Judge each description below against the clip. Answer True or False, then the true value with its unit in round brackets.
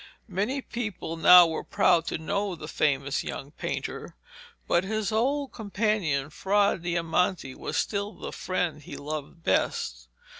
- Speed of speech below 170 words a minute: True (140 wpm)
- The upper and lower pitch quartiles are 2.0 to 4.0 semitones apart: False (4.9 semitones)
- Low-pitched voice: False (180 Hz)